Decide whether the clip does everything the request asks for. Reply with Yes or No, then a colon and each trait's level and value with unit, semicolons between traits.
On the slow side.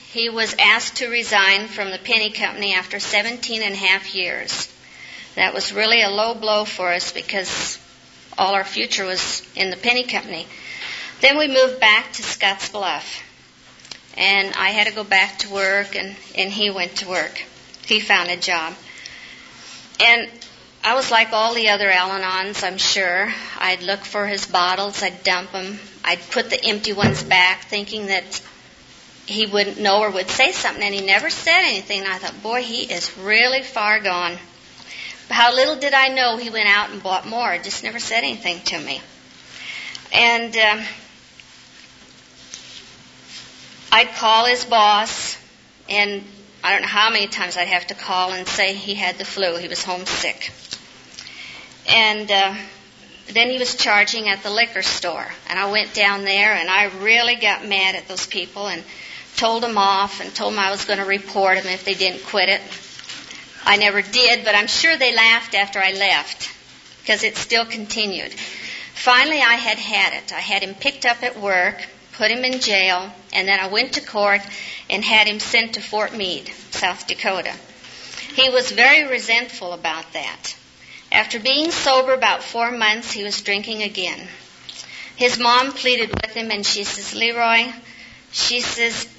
No: average, 175 wpm